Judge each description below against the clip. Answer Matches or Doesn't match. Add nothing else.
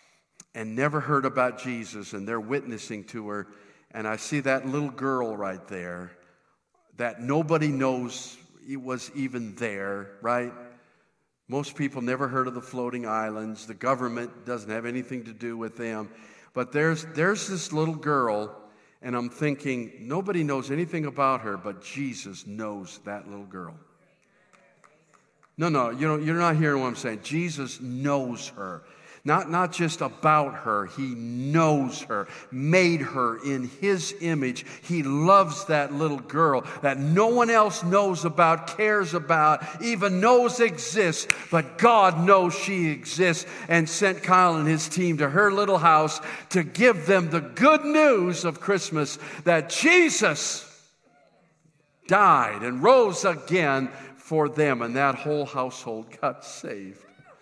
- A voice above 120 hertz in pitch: Matches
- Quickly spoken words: Doesn't match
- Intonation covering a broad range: Matches